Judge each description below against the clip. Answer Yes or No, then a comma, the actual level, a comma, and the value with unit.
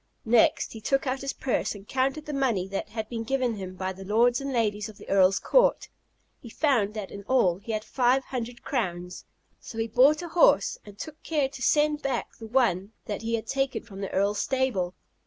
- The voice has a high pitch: Yes, high, 230 Hz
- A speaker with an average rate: No, fast, 215 wpm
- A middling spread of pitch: Yes, average, 4.8 semitones